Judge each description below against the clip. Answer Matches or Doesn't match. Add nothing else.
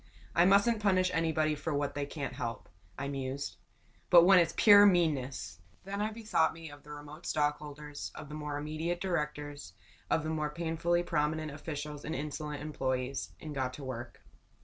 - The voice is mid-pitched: Matches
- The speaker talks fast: Doesn't match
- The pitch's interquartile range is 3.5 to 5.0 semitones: Doesn't match